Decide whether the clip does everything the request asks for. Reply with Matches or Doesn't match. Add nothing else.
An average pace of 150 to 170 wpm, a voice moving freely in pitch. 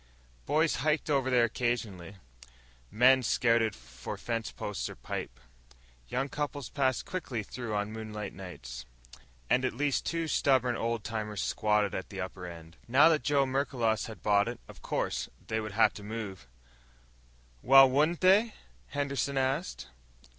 Doesn't match